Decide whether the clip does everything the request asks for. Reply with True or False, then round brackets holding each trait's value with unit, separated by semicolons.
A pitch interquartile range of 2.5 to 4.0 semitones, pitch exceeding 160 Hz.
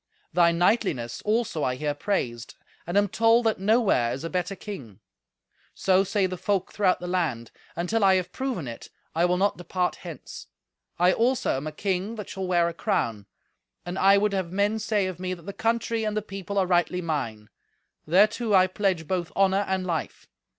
True (3.3 semitones; 185 Hz)